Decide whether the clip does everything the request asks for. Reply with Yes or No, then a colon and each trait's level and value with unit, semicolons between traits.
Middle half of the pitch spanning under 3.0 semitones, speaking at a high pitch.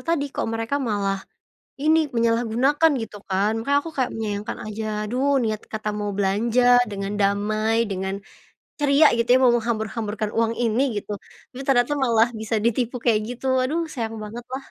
No: average, 3.3 semitones; high, 230 Hz